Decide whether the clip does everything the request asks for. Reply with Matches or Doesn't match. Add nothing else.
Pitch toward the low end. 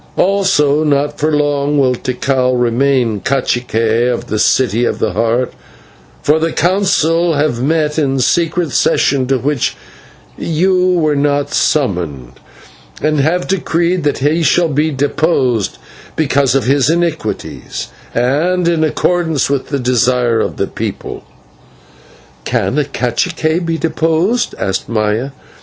Doesn't match